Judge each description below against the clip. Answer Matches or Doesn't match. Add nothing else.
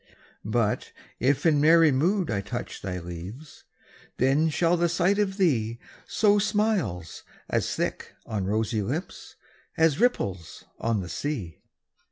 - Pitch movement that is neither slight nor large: Doesn't match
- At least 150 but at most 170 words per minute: Doesn't match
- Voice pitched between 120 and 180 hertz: Matches